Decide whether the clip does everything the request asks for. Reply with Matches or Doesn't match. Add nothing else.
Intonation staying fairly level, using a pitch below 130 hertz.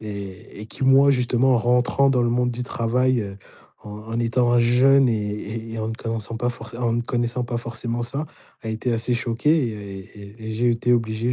Matches